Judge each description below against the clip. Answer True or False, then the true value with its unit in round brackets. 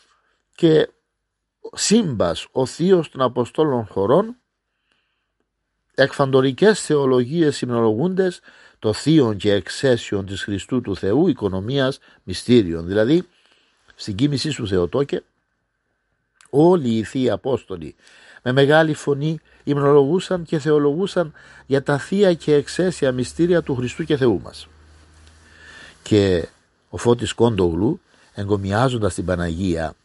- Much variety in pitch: True (7.2 semitones)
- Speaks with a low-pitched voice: True (130 Hz)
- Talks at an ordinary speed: False (105 wpm)